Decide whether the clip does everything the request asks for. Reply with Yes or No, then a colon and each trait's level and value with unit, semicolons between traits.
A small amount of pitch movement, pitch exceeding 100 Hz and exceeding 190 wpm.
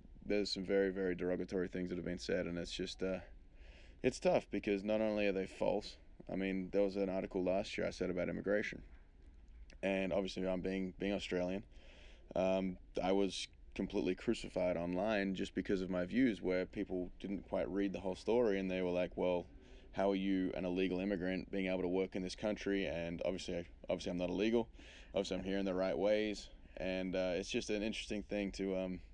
No: narrow, 1.7 semitones; very low, 95 Hz; fast, 205 wpm